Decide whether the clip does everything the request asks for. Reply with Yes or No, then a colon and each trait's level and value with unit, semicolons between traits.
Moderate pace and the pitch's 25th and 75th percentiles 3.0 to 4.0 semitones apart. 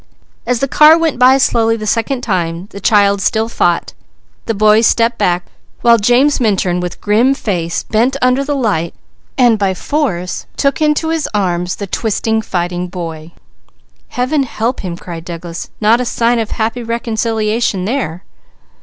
No: average, 160 wpm; average, 5.3 semitones